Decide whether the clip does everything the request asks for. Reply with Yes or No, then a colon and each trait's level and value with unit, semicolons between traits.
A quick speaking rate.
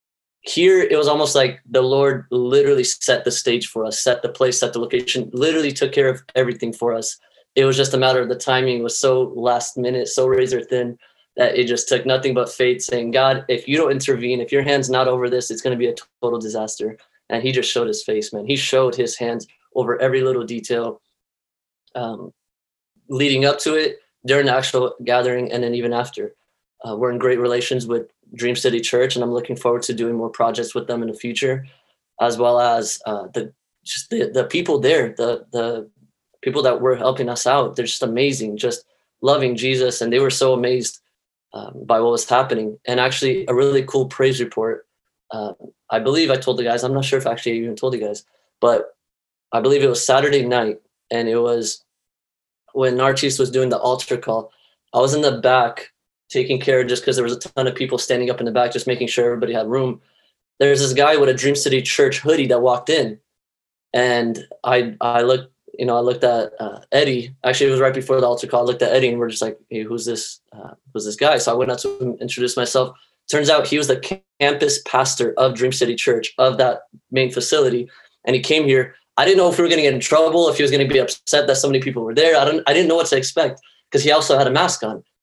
Yes: fast, 235 wpm